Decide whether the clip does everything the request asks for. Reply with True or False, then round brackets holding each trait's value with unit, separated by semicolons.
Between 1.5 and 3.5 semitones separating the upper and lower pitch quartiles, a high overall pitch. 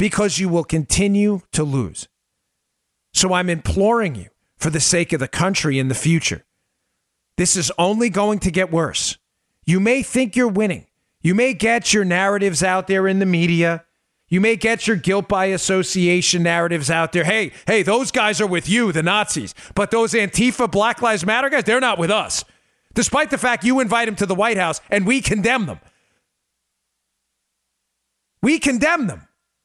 False (5.0 semitones; 195 Hz)